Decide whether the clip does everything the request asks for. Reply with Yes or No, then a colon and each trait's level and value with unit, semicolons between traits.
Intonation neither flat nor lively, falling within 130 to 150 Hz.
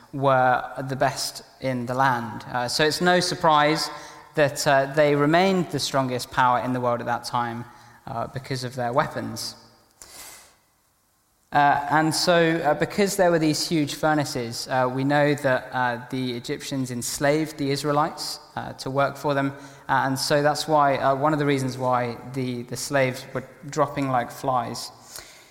Yes: average, 3.1 semitones; medium, 140 Hz